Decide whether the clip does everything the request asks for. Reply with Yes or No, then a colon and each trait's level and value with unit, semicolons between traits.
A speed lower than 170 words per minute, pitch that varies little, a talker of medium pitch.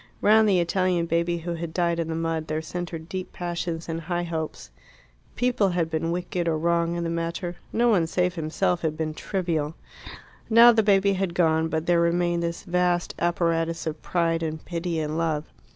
No: average, 190 wpm; narrow, 1.5 semitones; medium, 170 Hz